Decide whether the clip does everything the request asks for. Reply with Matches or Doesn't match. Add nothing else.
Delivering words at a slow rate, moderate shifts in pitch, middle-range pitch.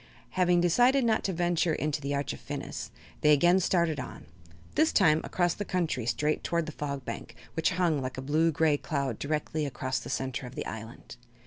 Doesn't match